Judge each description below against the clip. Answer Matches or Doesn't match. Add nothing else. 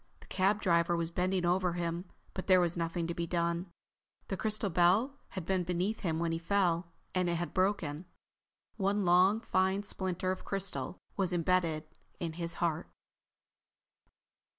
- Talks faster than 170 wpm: Doesn't match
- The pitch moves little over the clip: Matches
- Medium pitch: Matches